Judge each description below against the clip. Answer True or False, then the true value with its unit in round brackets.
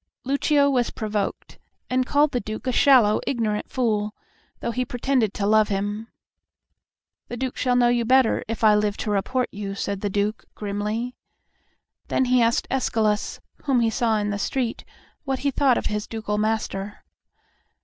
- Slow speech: False (170 wpm)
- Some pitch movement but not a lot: True (3.3 semitones)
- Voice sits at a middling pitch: False (225 Hz)